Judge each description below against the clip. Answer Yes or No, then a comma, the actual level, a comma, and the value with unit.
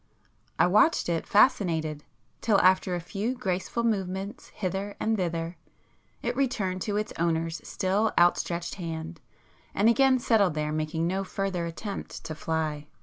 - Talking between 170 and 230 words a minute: No, average, 145 wpm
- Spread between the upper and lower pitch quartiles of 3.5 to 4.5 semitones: Yes, average, 4.1 semitones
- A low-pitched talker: No, medium, 185 Hz